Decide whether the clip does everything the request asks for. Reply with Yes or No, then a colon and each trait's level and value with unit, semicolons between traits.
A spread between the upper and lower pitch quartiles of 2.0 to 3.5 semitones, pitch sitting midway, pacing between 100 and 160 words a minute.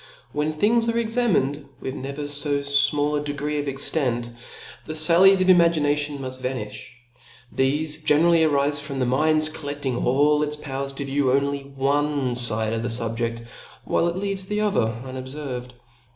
Yes: average, 2.7 semitones; medium, 145 Hz; average, 155 wpm